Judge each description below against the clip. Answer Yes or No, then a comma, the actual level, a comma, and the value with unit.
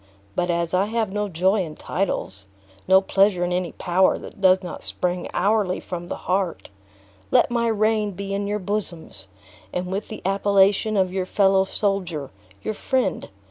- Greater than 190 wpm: No, average, 170 wpm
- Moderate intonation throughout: No, narrow, 2.3 semitones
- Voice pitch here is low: No, high, 190 Hz